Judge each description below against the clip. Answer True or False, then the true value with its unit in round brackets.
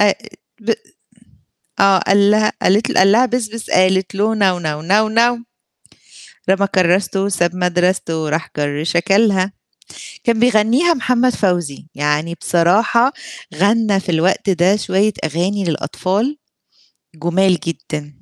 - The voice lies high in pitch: True (195 Hz)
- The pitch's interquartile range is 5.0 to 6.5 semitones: False (3.8 semitones)